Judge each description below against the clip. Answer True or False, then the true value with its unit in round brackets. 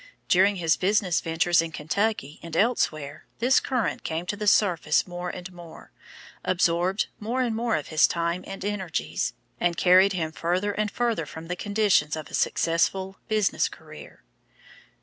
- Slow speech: False (160 wpm)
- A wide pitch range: False (3.8 semitones)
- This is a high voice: False (180 Hz)